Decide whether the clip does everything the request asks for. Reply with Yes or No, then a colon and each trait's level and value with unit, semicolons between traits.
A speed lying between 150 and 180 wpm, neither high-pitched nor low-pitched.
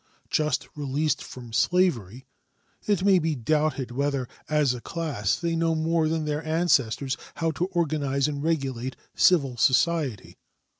No: average, 140 wpm; medium, 150 Hz